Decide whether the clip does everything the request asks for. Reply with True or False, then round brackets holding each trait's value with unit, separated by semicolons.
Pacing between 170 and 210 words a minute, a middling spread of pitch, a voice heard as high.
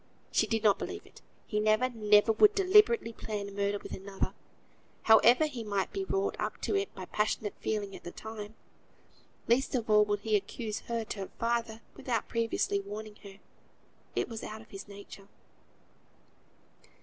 False (175 wpm; 2.3 semitones; 215 Hz)